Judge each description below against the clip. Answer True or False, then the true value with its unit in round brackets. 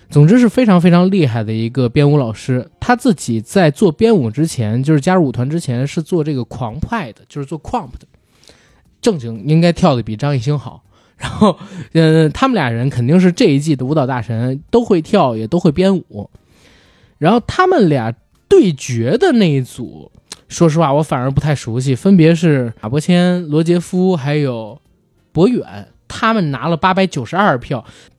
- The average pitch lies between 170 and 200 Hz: False (150 Hz)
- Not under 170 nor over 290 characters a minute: True (270 characters per minute)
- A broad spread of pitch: True (6.2 semitones)